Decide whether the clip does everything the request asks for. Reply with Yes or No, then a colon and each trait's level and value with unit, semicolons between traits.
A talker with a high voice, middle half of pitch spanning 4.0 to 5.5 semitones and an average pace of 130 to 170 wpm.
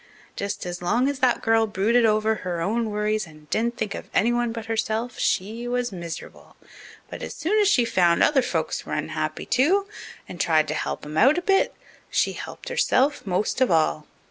No: high, 220 Hz; average, 5.1 semitones; average, 195 wpm